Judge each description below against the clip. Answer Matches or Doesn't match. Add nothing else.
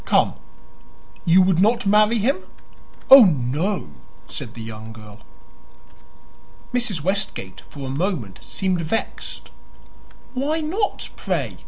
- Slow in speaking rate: Matches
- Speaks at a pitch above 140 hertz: Matches